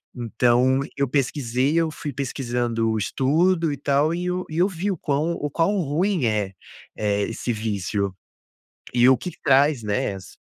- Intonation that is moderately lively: No, wide, 5.7 semitones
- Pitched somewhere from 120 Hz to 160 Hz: Yes, low, 135 Hz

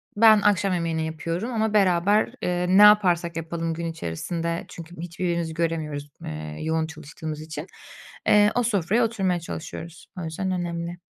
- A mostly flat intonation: No, average, 3.0 semitones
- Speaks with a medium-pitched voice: Yes, medium, 170 Hz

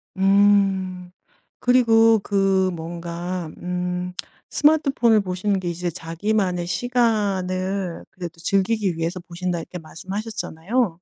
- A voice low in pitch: No, medium, 185 Hz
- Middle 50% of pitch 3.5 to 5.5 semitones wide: No, average, 2.9 semitones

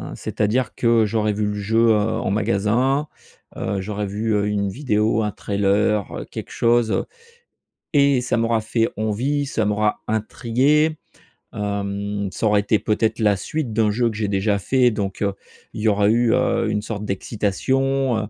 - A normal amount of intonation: No, narrow, 2.3 semitones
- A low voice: Yes, low, 110 Hz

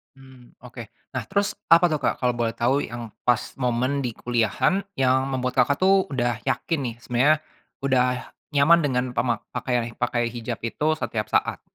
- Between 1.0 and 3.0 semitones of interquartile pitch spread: Yes, average, 2.7 semitones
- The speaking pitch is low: Yes, low, 125 Hz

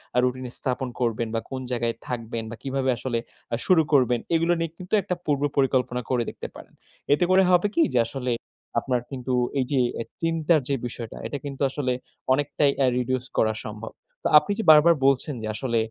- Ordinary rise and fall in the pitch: Yes, average, 3.3 semitones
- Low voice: Yes, low, 130 Hz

